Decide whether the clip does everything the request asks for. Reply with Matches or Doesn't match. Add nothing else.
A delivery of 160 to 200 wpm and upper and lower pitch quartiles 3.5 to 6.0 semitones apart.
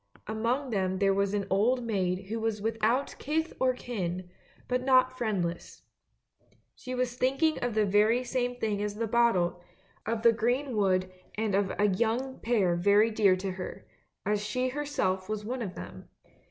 Matches